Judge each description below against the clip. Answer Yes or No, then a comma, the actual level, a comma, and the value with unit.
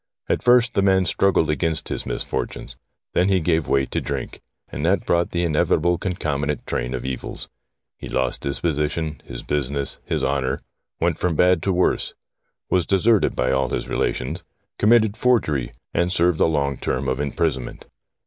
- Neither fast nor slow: Yes, average, 170 wpm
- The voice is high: No, very low, 80 Hz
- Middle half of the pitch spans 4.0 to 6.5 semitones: Yes, average, 4.7 semitones